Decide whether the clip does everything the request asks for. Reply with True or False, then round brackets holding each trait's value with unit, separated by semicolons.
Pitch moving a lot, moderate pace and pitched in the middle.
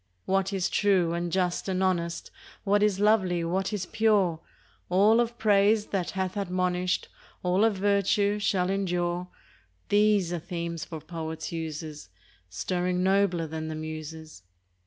False (2.9 semitones; 150 wpm; 180 Hz)